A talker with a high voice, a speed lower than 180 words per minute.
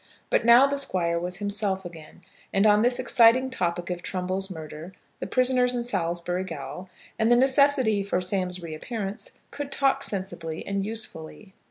Yes: high, 195 Hz; average, 160 wpm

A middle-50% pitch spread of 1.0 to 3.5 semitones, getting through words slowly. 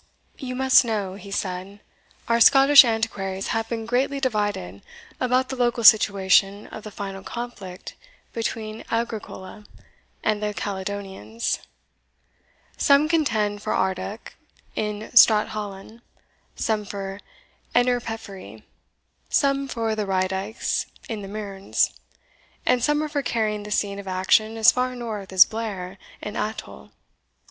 Yes: average, 3.2 semitones; slow, 125 wpm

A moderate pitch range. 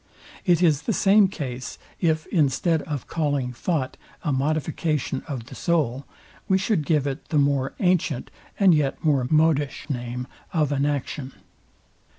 Yes: average, 3.4 semitones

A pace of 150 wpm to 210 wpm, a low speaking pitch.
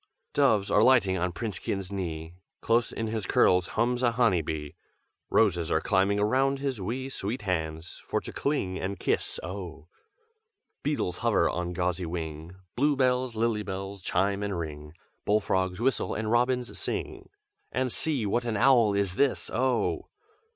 Yes: average, 160 wpm; low, 100 Hz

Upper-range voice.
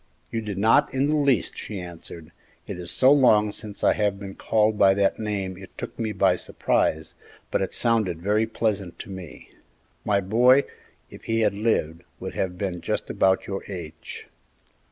No: low, 100 Hz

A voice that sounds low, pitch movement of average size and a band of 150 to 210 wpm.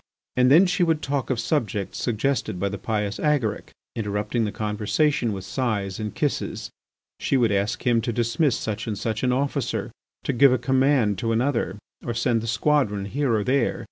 Yes: low, 115 Hz; average, 4.5 semitones; average, 185 wpm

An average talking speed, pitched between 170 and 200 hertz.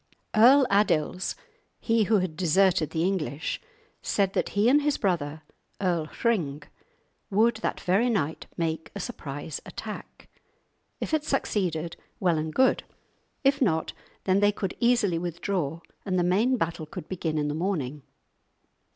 Yes: average, 145 wpm; medium, 185 Hz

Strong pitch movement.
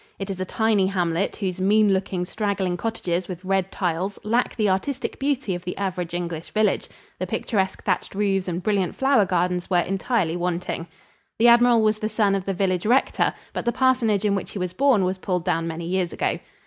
No: average, 3.1 semitones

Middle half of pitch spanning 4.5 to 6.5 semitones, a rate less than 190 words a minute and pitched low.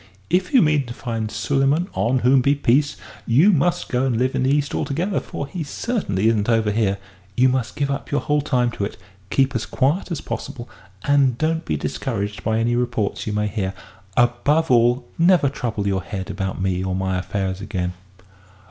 No: average, 5.3 semitones; average, 195 wpm; low, 125 Hz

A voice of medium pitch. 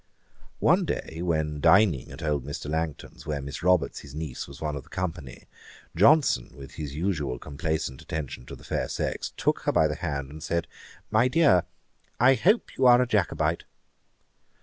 No: very low, 80 Hz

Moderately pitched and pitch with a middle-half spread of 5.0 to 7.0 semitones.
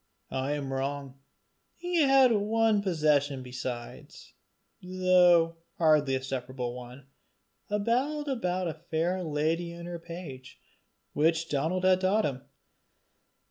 Yes: medium, 165 Hz; average, 5.3 semitones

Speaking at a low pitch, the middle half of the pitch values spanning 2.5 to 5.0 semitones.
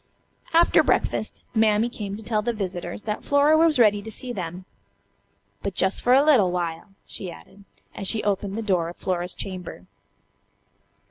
No: high, 205 Hz; average, 4.0 semitones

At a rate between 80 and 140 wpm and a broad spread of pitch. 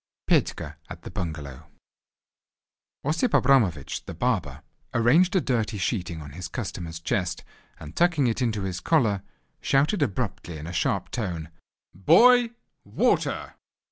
Yes: slow, 135 wpm; wide, 8.4 semitones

